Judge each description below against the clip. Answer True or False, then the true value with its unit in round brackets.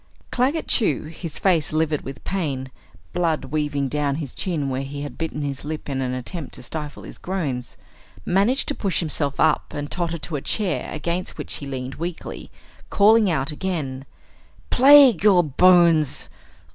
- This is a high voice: False (155 Hz)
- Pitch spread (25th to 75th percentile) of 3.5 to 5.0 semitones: True (4.4 semitones)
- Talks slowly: False (165 wpm)